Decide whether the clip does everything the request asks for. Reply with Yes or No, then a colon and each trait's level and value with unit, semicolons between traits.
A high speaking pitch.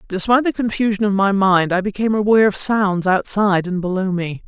Yes: high, 200 Hz